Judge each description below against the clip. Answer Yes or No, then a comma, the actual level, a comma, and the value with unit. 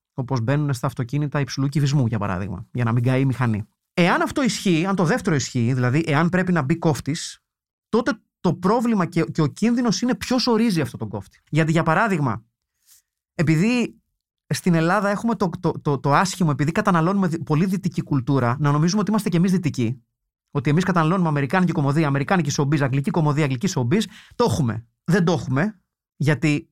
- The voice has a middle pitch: Yes, medium, 160 Hz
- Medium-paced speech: No, fast, 180 wpm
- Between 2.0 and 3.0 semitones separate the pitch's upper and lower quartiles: No, average, 5.3 semitones